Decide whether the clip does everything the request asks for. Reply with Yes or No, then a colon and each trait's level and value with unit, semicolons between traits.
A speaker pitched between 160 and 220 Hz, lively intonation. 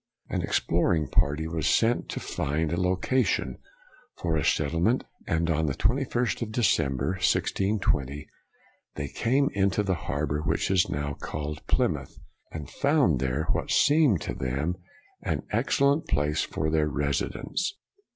No: very low, 80 Hz; wide, 6.6 semitones